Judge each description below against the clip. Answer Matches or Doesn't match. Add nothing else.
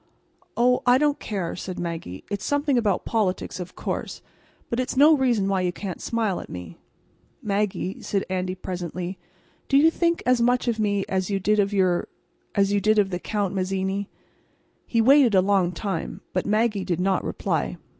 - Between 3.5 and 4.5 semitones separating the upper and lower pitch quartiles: Matches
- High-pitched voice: Matches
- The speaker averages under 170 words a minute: Doesn't match